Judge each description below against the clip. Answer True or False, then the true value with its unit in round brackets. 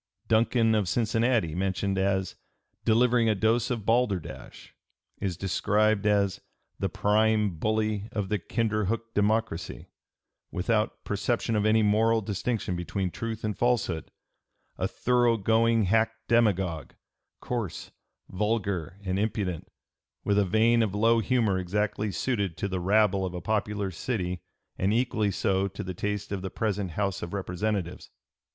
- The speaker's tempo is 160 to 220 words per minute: False (140 wpm)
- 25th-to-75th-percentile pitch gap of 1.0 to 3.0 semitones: True (2.7 semitones)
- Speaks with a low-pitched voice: True (105 Hz)